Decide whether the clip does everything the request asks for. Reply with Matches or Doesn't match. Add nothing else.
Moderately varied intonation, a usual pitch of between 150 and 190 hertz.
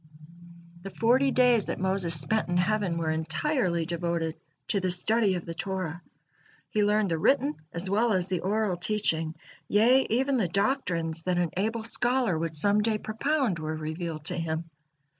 Matches